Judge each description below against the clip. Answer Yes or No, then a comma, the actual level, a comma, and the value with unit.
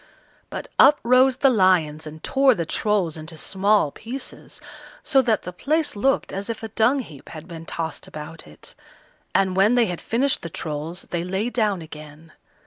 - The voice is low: No, high, 190 Hz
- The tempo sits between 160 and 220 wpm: Yes, average, 180 wpm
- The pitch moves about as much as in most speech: No, wide, 6.7 semitones